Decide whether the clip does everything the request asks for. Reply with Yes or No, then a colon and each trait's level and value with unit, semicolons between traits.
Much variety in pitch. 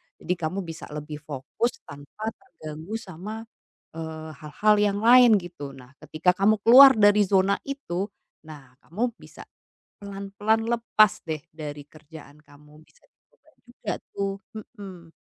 Yes: wide, 5.7 semitones